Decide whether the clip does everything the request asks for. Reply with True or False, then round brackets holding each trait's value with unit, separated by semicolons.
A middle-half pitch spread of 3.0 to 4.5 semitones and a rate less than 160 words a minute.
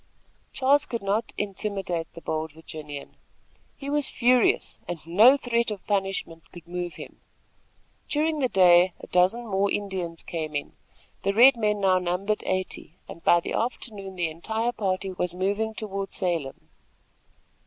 True (4.2 semitones; 150 wpm)